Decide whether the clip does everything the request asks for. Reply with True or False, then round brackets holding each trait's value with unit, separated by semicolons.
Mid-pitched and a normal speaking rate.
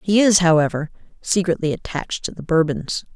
True (170 Hz; 150 wpm)